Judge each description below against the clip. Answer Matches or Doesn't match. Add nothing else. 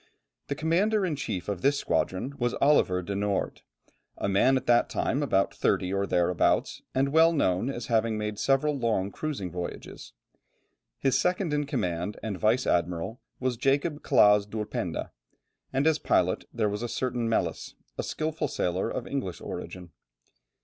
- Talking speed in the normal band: Matches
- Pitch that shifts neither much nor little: Doesn't match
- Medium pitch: Doesn't match